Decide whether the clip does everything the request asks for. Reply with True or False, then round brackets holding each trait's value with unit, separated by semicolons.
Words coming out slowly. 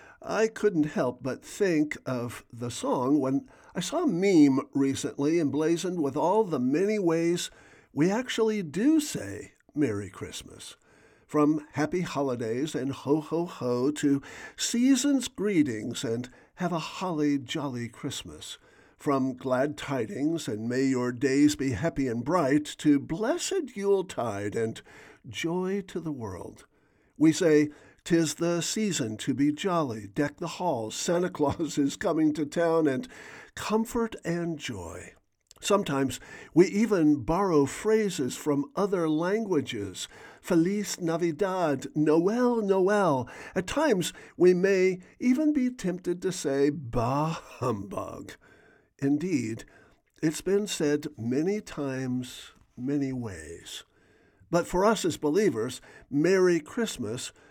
True (125 wpm)